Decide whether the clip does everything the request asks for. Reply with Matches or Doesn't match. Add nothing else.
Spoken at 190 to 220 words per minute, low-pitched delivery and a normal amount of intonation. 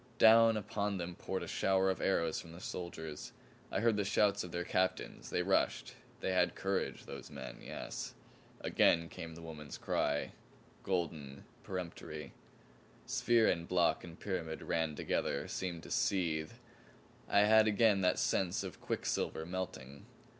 Doesn't match